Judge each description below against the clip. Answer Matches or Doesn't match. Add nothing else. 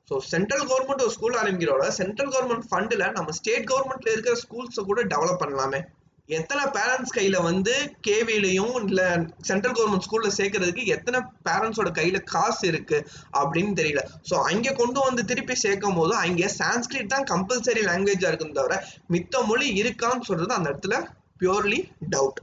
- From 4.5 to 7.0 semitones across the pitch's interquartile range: Matches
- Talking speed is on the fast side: Matches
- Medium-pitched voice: Doesn't match